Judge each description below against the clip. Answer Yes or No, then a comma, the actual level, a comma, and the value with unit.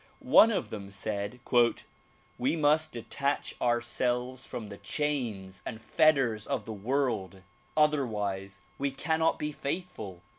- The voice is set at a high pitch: No, low, 120 Hz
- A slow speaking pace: Yes, slow, 120 wpm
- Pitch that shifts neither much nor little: No, wide, 6.2 semitones